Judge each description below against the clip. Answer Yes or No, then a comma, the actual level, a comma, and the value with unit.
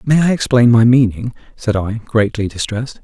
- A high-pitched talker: No, low, 115 Hz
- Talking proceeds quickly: No, average, 180 wpm